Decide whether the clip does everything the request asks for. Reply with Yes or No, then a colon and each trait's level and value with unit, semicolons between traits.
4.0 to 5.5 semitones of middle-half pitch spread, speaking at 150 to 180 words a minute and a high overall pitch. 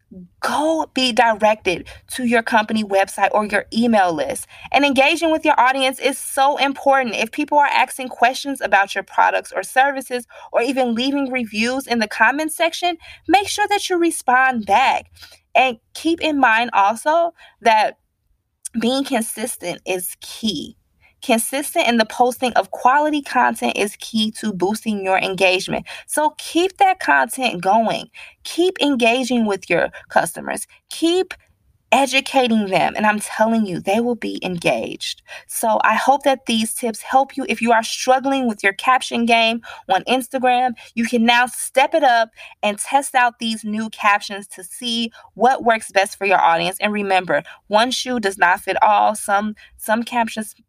Yes: average, 4.3 semitones; average, 160 wpm; high, 235 Hz